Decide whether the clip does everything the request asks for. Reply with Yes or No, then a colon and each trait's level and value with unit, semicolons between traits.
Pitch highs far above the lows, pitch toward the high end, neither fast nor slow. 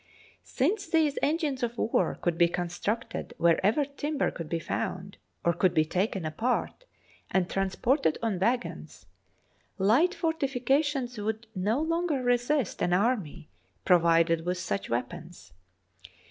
No: wide, 7.8 semitones; high, 220 Hz; slow, 130 wpm